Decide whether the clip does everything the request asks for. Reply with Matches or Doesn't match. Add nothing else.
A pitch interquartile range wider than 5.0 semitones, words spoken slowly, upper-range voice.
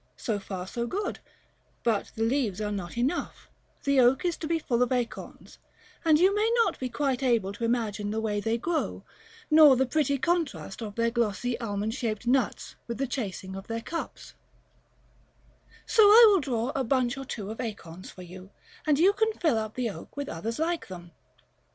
Doesn't match